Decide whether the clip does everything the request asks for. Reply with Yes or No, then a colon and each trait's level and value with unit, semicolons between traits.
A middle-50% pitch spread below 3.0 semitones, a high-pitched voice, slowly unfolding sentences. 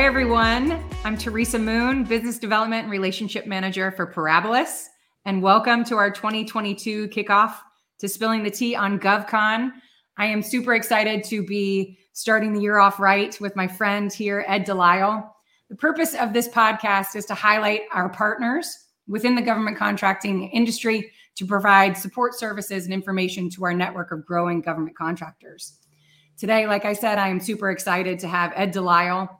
No: narrow, 2.6 semitones; high, 205 Hz; average, 165 wpm